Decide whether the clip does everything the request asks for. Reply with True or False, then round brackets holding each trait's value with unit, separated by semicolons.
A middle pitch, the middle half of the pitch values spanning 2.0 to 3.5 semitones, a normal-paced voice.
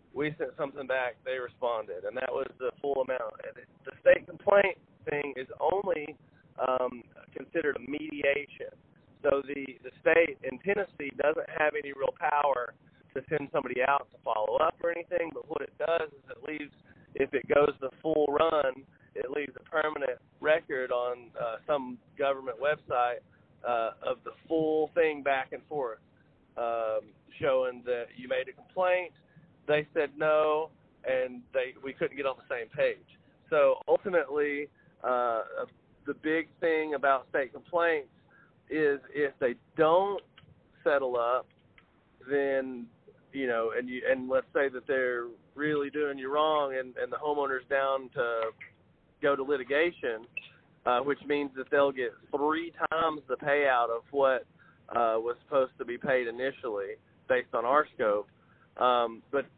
False (145 Hz; 4.4 semitones; 155 wpm)